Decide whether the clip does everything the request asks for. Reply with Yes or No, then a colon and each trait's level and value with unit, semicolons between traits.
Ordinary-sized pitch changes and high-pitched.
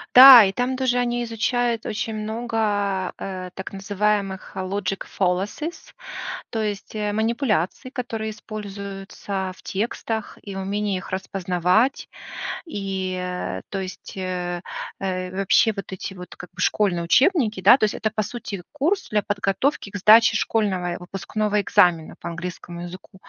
Yes: average, 3.0 semitones; high, 200 Hz